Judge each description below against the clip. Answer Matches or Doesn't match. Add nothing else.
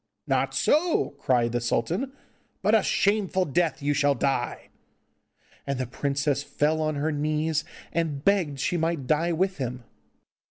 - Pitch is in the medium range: Matches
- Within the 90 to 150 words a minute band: Matches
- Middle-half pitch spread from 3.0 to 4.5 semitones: Matches